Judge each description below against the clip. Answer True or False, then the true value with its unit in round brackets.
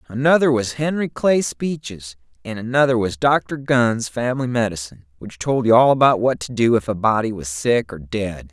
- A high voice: False (115 Hz)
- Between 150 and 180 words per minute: False (190 wpm)